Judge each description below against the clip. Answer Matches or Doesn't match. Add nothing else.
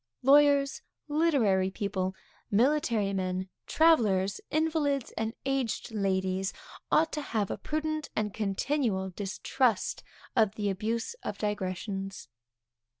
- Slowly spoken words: Matches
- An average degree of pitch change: Doesn't match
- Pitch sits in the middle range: Doesn't match